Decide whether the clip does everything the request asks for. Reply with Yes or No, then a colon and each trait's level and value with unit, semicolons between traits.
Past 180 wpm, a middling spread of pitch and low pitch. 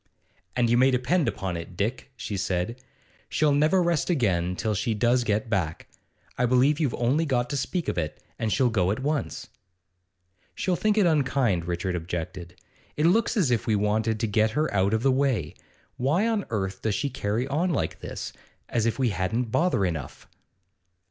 No: average, 190 wpm; wide, 6.4 semitones; low, 120 Hz